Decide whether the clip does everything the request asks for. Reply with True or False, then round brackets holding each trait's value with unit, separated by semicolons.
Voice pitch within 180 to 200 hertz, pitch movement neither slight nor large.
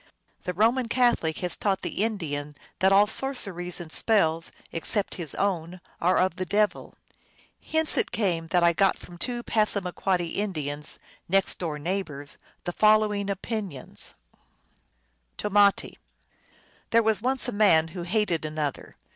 True (190 Hz; 4.3 semitones)